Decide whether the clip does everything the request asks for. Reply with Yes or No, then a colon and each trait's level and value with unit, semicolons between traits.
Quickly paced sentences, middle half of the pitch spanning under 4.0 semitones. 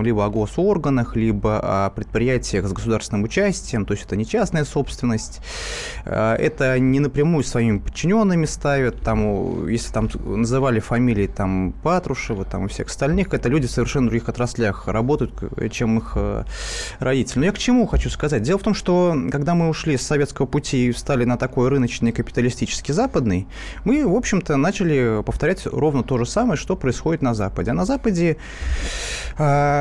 No: fast, 165 wpm; average, 5.1 semitones